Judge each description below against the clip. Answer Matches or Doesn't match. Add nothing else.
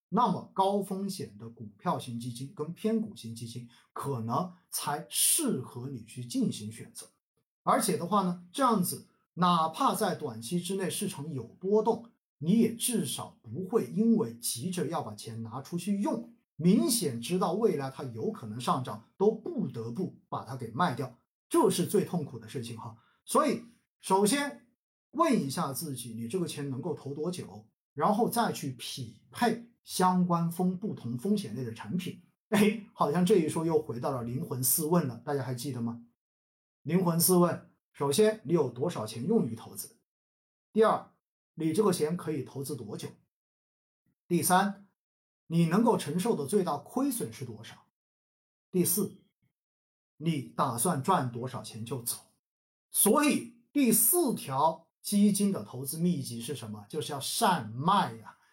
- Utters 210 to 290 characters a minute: Matches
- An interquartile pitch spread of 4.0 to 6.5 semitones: Doesn't match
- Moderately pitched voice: Matches